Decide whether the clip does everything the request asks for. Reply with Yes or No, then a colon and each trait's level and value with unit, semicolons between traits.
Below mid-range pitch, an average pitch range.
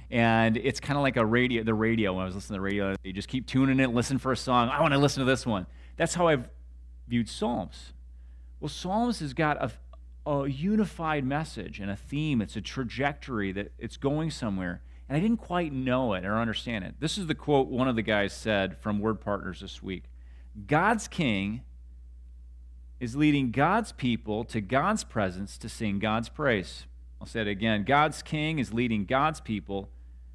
No: low, 115 Hz; wide, 6.4 semitones